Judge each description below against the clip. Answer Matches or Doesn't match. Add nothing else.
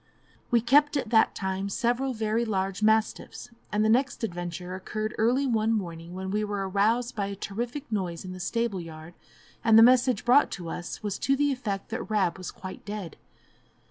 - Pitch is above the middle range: Matches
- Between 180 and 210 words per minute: Matches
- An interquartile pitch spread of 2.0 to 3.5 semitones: Doesn't match